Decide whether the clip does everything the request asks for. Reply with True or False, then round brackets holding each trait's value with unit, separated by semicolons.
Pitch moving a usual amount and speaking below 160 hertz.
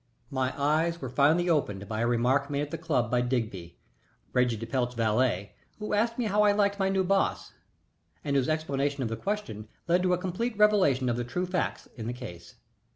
False (7.2 semitones; 140 Hz)